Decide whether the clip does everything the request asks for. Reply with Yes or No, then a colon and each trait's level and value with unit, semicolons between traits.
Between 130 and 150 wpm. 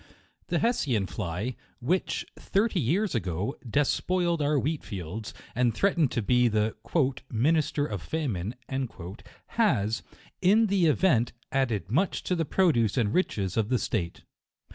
Yes: average, 140 wpm